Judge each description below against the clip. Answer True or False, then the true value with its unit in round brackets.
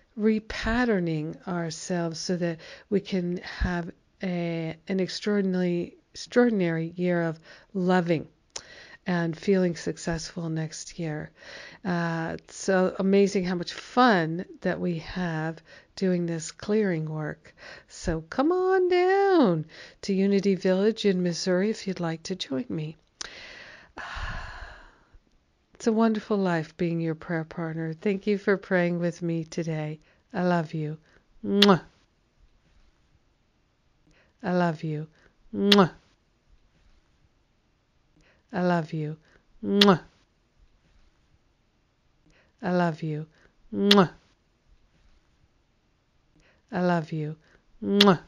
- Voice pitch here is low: False (180 Hz)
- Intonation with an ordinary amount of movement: True (3.3 semitones)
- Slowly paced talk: True (100 wpm)